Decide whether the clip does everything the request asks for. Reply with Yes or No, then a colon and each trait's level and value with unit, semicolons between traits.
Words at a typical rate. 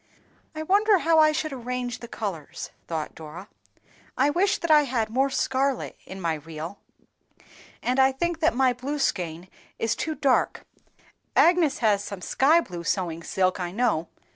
Yes: average, 165 wpm